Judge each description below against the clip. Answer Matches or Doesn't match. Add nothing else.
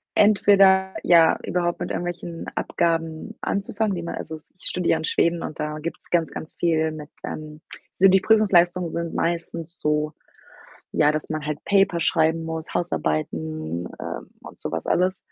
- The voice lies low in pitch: Doesn't match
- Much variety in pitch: Doesn't match